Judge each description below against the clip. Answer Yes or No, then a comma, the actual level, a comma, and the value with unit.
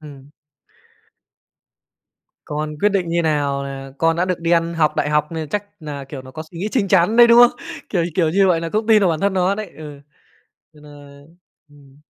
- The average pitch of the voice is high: No, medium, 165 Hz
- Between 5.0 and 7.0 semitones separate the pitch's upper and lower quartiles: No, average, 4.4 semitones